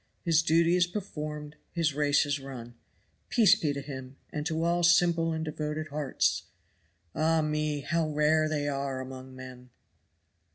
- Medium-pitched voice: Yes, medium, 150 Hz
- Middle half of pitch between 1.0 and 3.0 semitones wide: Yes, average, 2.7 semitones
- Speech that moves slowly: No, average, 155 wpm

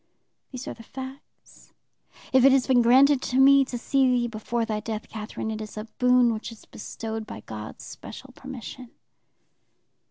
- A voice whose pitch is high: Yes, high, 245 Hz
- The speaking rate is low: No, average, 170 wpm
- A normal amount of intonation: Yes, average, 3.1 semitones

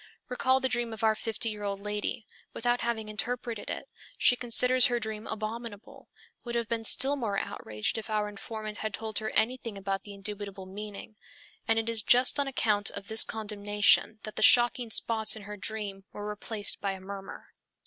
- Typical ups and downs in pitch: No, narrow, 2.1 semitones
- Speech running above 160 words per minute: Yes, average, 190 wpm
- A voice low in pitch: No, high, 220 Hz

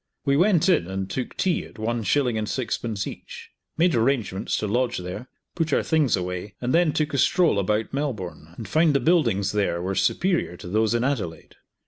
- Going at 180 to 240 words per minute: Yes, average, 195 wpm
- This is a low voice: Yes, low, 115 Hz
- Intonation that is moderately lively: No, wide, 7.1 semitones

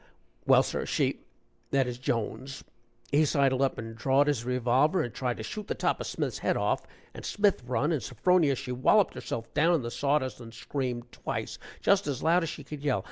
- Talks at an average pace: No, fast, 210 wpm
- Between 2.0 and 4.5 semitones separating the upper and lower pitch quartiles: Yes, average, 3.6 semitones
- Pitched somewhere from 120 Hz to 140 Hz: Yes, low, 135 Hz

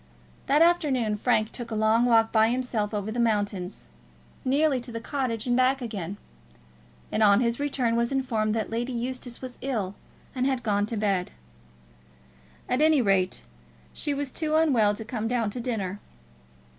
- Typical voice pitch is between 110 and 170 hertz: No, high, 235 Hz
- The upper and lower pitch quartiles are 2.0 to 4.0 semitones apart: Yes, average, 3.2 semitones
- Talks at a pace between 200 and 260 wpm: No, average, 170 wpm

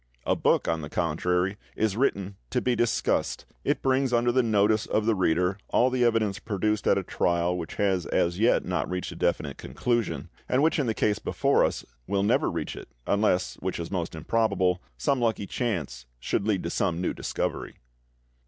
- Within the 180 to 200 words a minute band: Yes, average, 190 wpm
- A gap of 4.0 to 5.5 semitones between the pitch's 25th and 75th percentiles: Yes, average, 4.3 semitones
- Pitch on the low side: Yes, low, 100 Hz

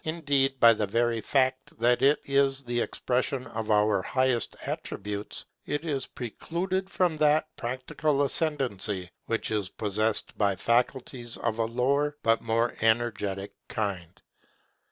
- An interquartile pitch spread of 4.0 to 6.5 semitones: Yes, average, 4.3 semitones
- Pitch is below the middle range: Yes, low, 120 Hz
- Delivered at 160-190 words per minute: No, slow, 135 wpm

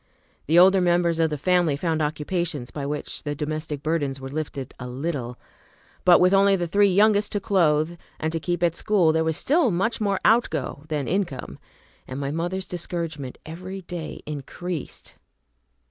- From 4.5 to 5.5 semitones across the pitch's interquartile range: No, average, 3.7 semitones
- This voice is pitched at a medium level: Yes, medium, 165 Hz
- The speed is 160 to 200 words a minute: Yes, average, 170 wpm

